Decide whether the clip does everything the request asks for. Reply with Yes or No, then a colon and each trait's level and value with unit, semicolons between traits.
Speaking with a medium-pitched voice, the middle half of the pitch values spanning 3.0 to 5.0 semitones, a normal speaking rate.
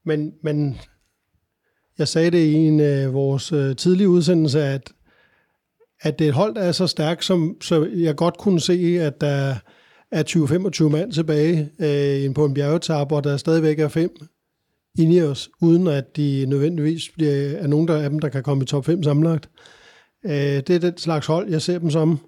No: medium, 155 Hz; narrow, 2.4 semitones; average, 190 wpm